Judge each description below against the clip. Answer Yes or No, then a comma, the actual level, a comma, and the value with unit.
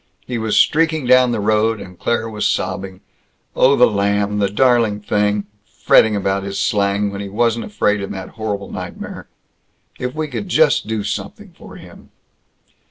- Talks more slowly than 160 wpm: No, average, 165 wpm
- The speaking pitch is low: Yes, low, 105 Hz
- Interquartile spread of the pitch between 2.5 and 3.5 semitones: Yes, average, 3.2 semitones